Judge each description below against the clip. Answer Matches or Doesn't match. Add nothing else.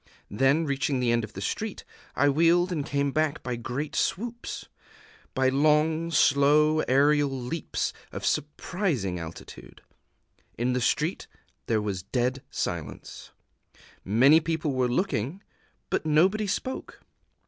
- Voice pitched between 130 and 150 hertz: Matches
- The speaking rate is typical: Doesn't match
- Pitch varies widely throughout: Doesn't match